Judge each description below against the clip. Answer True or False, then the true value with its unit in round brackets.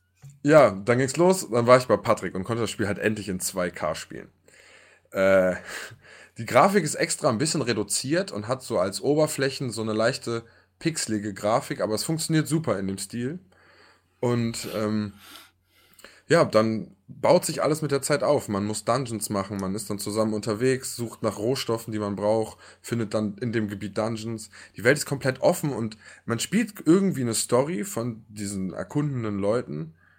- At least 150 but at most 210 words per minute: True (180 wpm)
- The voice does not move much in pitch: False (4.2 semitones)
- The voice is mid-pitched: False (115 Hz)